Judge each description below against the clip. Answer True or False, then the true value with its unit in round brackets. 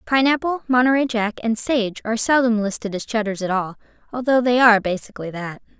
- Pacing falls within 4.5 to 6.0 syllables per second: True (5.9 syllables/s)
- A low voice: False (230 Hz)